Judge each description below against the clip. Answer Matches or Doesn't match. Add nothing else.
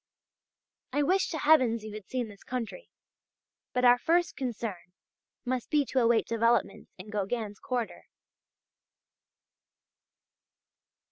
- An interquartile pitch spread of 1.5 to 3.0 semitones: Doesn't match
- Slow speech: Matches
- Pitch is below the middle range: Doesn't match